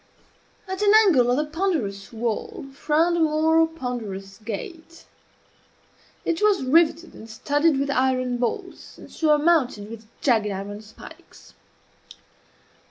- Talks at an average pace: No, slow, 120 wpm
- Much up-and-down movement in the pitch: Yes, wide, 6.5 semitones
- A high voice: Yes, very high, 275 Hz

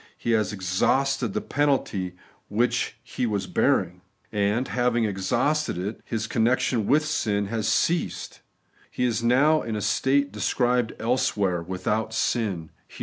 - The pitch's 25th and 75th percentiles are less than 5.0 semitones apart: Yes, average, 3.8 semitones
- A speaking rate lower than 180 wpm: Yes, average, 140 wpm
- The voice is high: No, low, 115 Hz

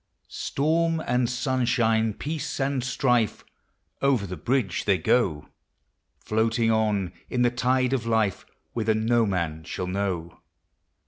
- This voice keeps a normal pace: No, slow, 125 wpm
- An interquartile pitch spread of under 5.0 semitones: Yes, average, 4.1 semitones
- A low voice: Yes, low, 115 Hz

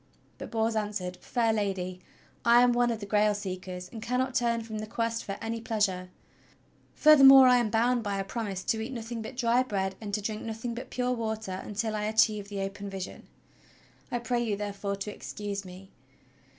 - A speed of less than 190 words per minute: No, average, 195 wpm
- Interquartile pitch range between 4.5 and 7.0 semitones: No, average, 2.8 semitones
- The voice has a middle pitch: No, high, 220 Hz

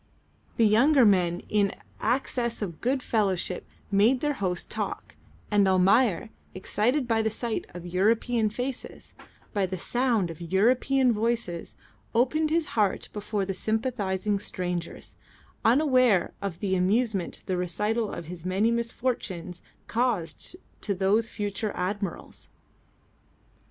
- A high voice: Yes, high, 210 Hz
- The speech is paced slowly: Yes, slow, 125 wpm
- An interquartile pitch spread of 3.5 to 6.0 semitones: Yes, average, 4.2 semitones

